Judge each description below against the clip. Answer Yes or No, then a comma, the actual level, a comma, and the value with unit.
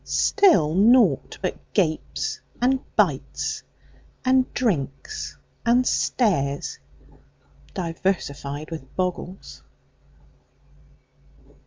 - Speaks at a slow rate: Yes, slow, 65 wpm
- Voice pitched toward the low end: No, medium, 185 Hz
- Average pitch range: No, wide, 8.3 semitones